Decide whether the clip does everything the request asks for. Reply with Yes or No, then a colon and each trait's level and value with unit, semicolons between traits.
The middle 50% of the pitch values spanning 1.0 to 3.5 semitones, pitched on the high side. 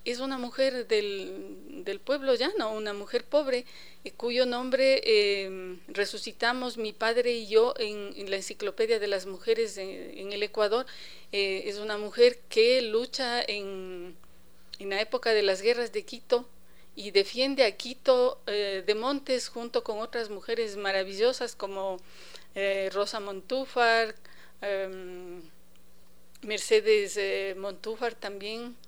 No: average, 4.1 semitones; high, 220 Hz